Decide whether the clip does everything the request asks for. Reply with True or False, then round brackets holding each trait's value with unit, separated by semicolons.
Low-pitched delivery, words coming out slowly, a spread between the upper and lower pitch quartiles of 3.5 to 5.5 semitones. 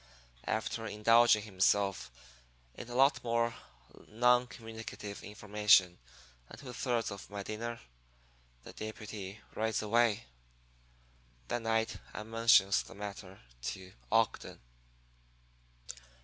False (110 Hz; 105 wpm; 2.4 semitones)